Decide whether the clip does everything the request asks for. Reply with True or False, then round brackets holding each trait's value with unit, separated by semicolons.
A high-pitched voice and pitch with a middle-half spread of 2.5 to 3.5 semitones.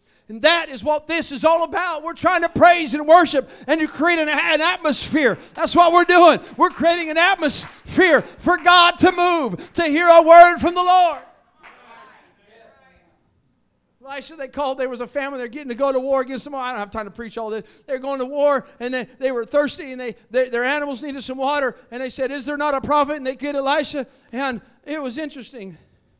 False (285 Hz; 4.3 semitones)